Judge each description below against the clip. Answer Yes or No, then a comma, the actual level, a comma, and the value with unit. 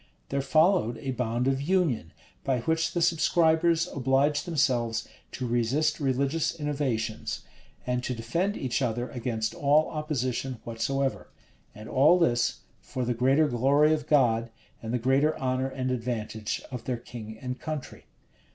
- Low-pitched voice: Yes, low, 130 Hz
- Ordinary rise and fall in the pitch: Yes, average, 4.1 semitones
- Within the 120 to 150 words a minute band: Yes, average, 145 wpm